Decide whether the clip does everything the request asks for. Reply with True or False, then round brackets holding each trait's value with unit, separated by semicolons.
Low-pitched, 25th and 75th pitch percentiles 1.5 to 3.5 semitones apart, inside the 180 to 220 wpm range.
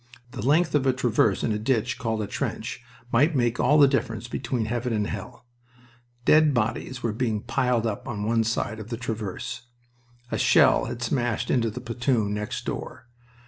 True (115 Hz; 2.5 semitones; 185 wpm)